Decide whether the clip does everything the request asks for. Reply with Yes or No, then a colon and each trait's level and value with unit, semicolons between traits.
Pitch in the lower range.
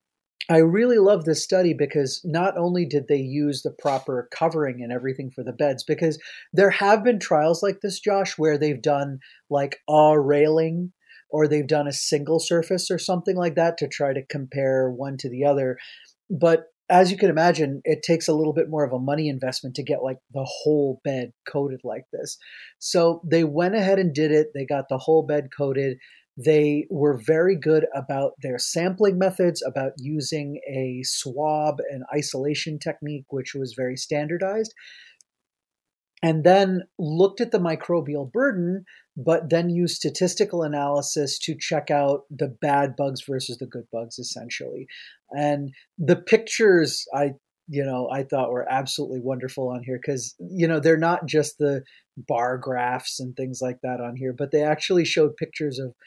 No: medium, 150 Hz